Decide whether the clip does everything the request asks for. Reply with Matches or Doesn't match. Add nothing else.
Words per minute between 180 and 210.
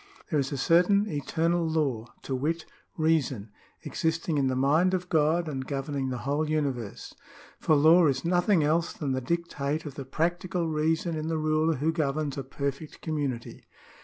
Matches